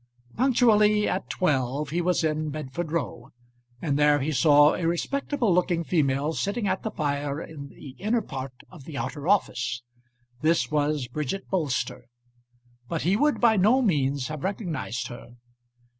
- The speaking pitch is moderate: Yes, medium, 155 Hz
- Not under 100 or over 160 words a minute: Yes, average, 155 wpm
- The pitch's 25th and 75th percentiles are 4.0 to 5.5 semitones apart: Yes, average, 5.2 semitones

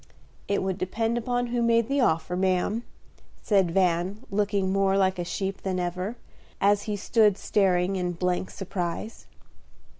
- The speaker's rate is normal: Yes, average, 150 wpm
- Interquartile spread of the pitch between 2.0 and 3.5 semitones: Yes, average, 2.8 semitones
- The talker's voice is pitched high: Yes, high, 195 Hz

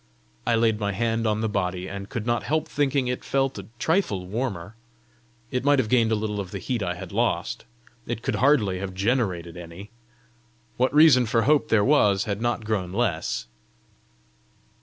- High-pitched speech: No, low, 110 Hz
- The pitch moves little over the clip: No, average, 4.4 semitones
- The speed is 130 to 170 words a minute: No, average, 180 wpm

